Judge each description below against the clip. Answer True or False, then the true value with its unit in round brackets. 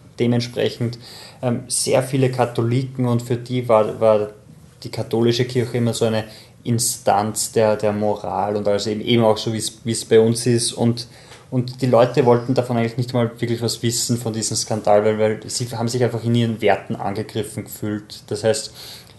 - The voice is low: True (115 Hz)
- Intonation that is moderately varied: False (2.1 semitones)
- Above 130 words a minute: True (185 wpm)